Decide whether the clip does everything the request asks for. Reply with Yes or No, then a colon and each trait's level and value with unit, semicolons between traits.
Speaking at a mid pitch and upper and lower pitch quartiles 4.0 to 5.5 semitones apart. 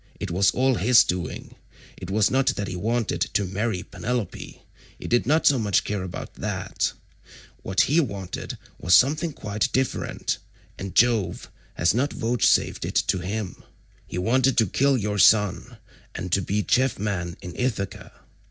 No: low, 105 Hz; average, 4.8 semitones